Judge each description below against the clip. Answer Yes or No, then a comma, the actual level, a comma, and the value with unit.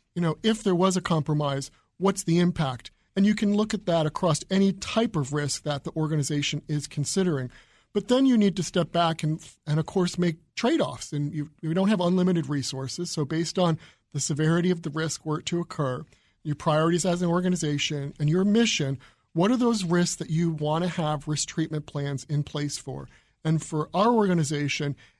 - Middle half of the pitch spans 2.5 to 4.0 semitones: Yes, average, 3.2 semitones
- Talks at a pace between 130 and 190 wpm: No, average, 200 wpm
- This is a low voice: No, medium, 160 Hz